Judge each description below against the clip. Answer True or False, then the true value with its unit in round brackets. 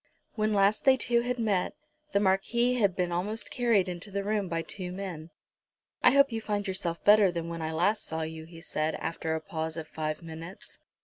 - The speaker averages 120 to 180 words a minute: False (205 wpm)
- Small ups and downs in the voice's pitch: False (4.4 semitones)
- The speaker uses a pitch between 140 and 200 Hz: True (190 Hz)